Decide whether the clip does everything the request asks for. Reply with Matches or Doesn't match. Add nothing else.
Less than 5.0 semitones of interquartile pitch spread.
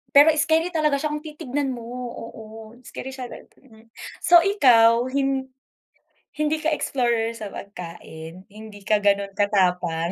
Doesn't match